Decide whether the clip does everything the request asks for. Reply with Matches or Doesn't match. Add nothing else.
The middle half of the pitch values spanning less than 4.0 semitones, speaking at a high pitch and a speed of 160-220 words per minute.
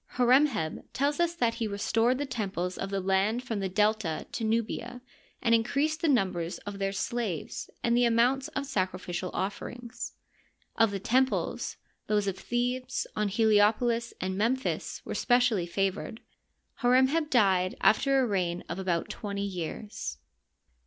Doesn't match